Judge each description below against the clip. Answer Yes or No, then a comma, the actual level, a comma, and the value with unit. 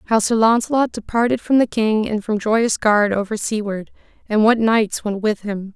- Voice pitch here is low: No, high, 215 Hz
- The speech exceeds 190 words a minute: Yes, average, 200 wpm